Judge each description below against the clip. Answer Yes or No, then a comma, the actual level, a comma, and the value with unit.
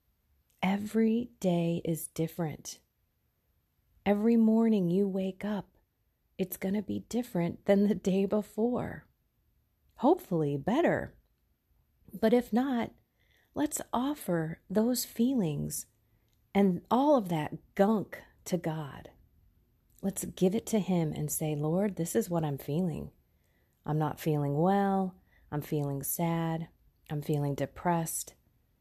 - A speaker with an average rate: No, slow, 120 wpm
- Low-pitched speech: No, medium, 175 Hz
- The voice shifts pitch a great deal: Yes, wide, 5.7 semitones